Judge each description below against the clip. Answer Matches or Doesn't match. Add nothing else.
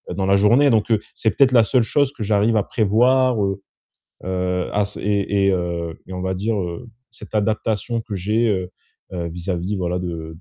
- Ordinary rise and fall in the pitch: Matches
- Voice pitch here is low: Matches